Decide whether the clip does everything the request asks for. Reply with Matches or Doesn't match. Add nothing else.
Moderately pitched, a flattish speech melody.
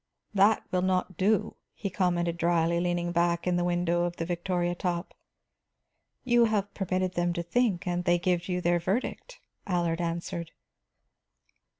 Matches